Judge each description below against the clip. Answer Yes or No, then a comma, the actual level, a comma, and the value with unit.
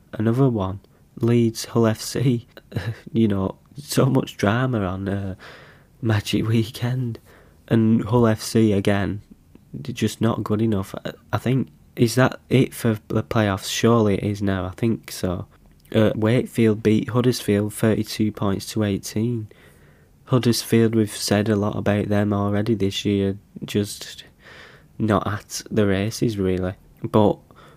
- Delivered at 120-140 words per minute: Yes, slow, 135 wpm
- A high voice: No, low, 105 Hz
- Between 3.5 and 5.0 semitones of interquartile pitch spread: No, narrow, 2.6 semitones